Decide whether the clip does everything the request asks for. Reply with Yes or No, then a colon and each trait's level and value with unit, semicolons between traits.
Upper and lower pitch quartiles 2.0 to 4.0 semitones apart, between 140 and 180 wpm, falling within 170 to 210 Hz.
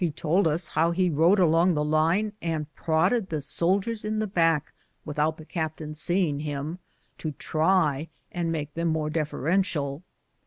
No: average, 2.9 semitones; average, 160 wpm; medium, 160 Hz